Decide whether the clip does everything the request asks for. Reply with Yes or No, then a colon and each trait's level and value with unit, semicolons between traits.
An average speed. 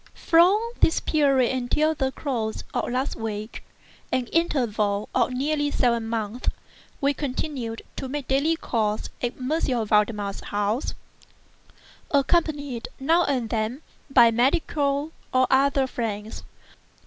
No: slow, 115 wpm